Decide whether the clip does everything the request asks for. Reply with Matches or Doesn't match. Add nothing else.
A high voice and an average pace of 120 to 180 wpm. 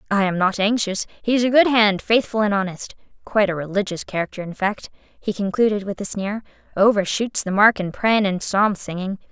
Doesn't match